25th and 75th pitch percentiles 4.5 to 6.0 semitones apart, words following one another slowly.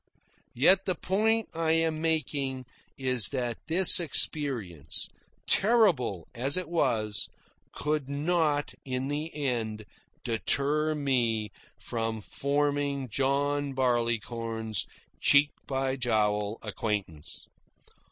Yes: average, 5.0 semitones; slow, 95 wpm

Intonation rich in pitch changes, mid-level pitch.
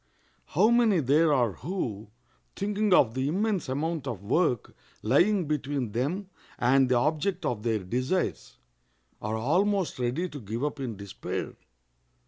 Yes: wide, 7.0 semitones; medium, 145 Hz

